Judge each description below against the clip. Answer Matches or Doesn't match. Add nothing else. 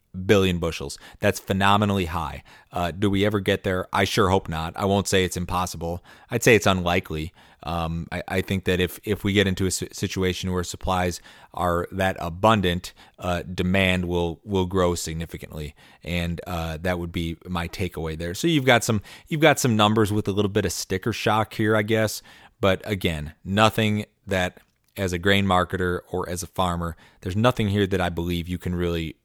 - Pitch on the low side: Matches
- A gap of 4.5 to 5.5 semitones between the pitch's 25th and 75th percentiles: Doesn't match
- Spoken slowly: Doesn't match